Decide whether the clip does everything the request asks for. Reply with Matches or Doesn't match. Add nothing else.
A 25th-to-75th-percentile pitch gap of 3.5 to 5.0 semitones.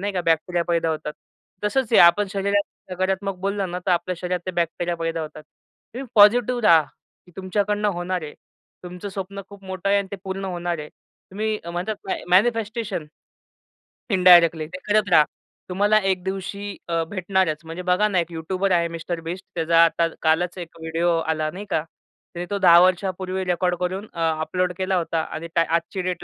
Doesn't match